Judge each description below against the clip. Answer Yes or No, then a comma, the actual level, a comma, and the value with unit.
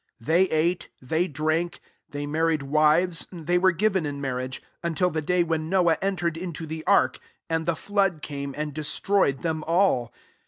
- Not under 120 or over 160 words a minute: No, average, 180 wpm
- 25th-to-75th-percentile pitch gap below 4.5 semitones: Yes, average, 2.9 semitones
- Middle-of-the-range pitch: Yes, medium, 160 Hz